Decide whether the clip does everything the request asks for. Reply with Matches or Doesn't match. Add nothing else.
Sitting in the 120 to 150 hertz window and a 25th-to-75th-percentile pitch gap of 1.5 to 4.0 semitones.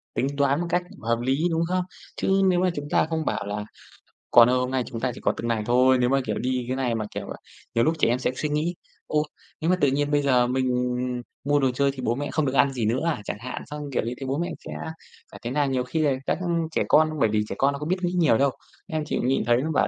Matches